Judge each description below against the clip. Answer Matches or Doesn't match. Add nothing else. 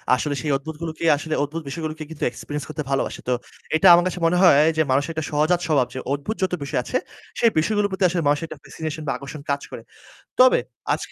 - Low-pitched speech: Doesn't match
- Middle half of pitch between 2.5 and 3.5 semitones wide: Matches